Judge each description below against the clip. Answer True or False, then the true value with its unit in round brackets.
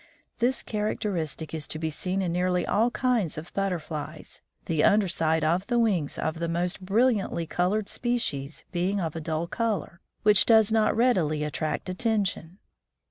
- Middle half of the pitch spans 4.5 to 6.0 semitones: True (5.0 semitones)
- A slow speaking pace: False (160 wpm)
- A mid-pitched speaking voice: True (180 Hz)